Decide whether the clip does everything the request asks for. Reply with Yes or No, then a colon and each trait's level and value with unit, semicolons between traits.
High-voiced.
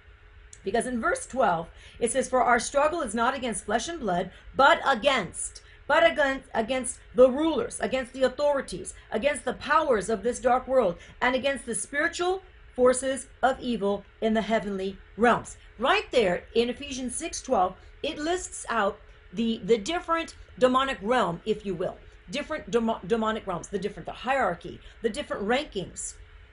Yes: high, 245 Hz